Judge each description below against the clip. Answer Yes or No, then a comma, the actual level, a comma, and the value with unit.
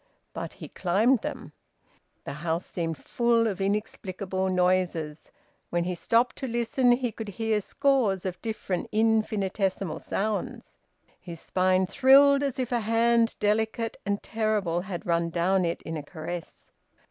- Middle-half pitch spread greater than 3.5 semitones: Yes, average, 4.2 semitones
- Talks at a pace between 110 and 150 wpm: Yes, average, 145 wpm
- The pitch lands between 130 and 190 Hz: No, high, 200 Hz